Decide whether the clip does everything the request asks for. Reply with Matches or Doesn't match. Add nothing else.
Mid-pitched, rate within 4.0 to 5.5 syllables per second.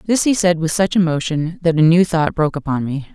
Doesn't match